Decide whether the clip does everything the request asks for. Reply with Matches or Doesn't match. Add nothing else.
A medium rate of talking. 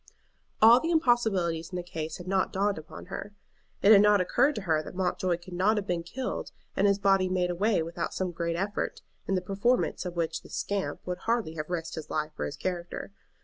Doesn't match